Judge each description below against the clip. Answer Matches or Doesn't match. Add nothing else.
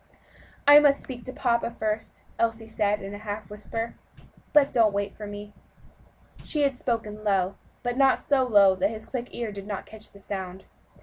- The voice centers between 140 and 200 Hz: Doesn't match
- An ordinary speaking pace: Matches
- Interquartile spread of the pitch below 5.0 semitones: Matches